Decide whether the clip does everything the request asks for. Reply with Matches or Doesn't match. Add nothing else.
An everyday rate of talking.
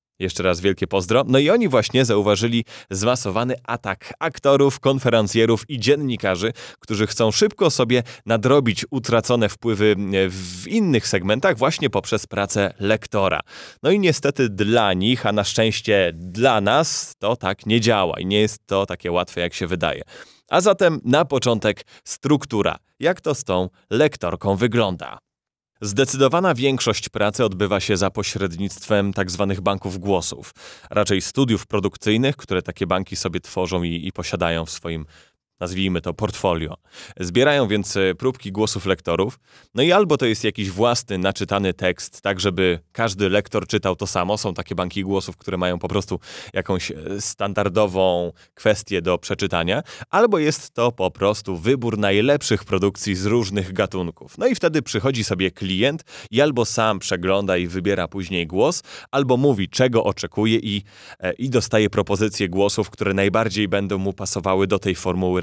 Matches